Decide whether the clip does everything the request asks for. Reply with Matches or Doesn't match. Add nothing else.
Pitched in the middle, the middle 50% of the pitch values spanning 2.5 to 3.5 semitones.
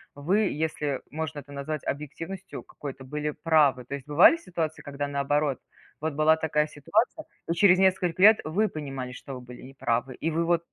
Matches